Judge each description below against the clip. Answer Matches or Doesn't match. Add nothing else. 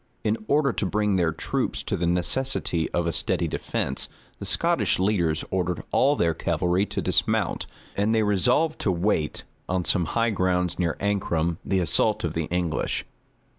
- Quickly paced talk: Doesn't match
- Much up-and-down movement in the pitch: Doesn't match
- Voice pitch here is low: Matches